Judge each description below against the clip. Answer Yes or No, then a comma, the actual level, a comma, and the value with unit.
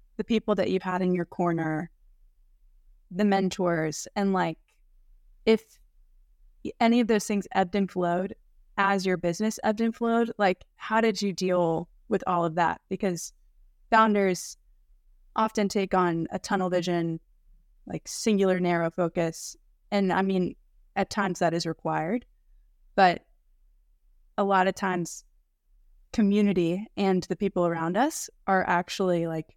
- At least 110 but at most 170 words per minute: Yes, average, 140 wpm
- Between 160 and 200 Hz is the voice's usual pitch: Yes, medium, 185 Hz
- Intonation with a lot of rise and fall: No, average, 3.2 semitones